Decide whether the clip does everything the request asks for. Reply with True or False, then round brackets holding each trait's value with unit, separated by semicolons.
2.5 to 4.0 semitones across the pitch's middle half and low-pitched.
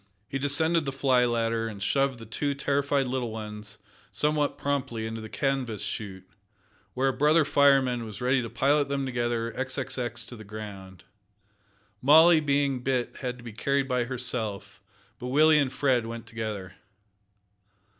True (3.6 semitones; 125 Hz)